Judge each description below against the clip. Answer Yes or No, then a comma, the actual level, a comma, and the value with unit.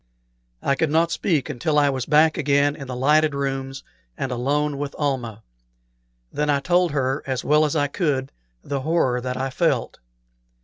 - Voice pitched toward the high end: No, medium, 140 Hz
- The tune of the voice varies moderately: No, narrow, 2.3 semitones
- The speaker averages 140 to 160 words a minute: No, average, 175 wpm